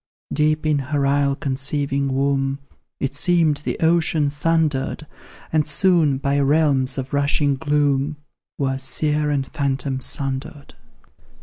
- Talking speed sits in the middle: No, slow, 120 wpm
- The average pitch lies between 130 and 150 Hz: Yes, medium, 140 Hz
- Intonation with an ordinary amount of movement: No, narrow, 1.8 semitones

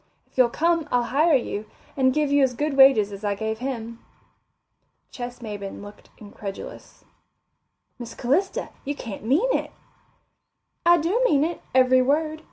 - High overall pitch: Yes, very high, 260 Hz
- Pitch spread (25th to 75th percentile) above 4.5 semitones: Yes, average, 5.3 semitones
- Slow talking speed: No, average, 155 wpm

